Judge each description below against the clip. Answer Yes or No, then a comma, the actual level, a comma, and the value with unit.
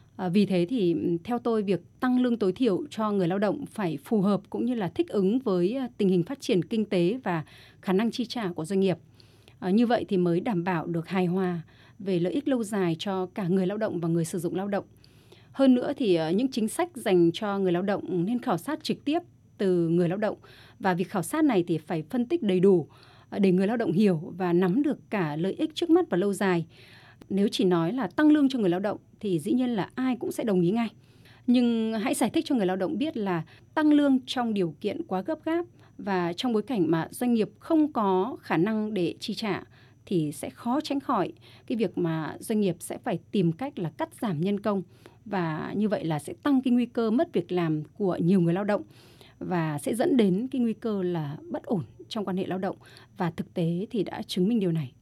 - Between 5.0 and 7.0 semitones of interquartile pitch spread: Yes, wide, 5.4 semitones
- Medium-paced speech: Yes, average, 240 wpm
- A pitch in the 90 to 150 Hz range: No, high, 190 Hz